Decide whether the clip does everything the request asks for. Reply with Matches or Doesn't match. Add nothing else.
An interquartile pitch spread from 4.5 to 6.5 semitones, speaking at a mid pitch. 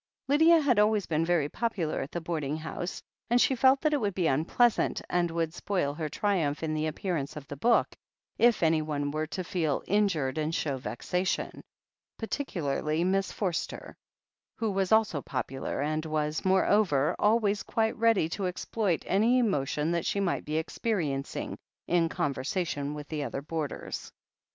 Matches